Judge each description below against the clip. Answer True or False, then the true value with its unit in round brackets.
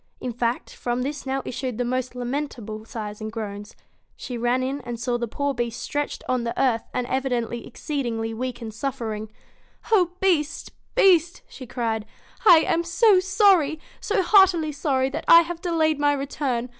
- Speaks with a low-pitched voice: False (260 Hz)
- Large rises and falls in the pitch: False (4.9 semitones)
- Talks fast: False (170 wpm)